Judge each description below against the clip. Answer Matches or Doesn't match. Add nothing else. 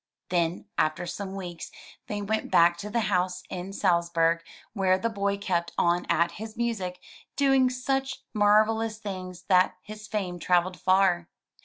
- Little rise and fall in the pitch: Doesn't match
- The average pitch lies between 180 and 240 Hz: Matches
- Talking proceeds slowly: Doesn't match